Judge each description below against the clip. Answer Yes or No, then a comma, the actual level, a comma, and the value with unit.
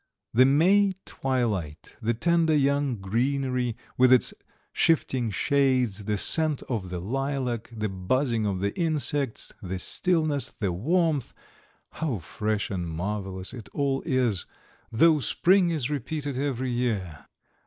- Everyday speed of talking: No, slow, 130 wpm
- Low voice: Yes, low, 125 Hz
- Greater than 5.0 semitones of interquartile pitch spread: Yes, wide, 5.5 semitones